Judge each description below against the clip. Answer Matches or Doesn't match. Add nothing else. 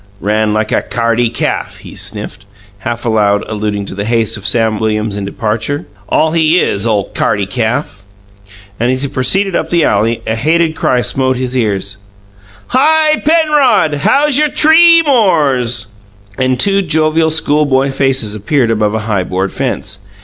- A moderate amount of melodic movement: Doesn't match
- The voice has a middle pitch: Doesn't match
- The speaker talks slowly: Doesn't match